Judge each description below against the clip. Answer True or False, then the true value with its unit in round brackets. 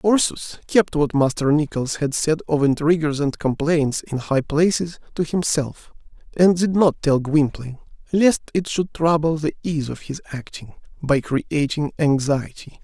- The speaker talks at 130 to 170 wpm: True (155 wpm)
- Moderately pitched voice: True (155 Hz)